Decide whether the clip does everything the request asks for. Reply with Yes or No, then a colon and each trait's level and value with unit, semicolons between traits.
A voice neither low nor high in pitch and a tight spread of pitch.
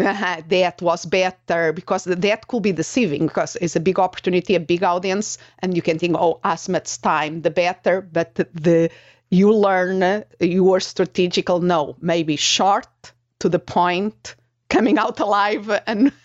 Yes: medium, 180 Hz; narrow, 2.1 semitones